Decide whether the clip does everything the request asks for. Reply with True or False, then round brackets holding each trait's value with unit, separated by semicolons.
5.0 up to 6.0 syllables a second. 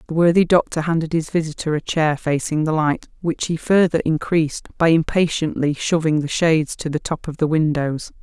True (5.4 syllables/s)